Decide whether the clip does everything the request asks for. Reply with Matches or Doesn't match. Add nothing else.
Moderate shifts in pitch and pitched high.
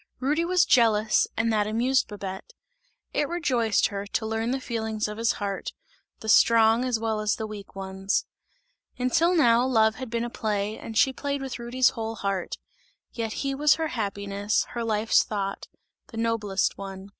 Matches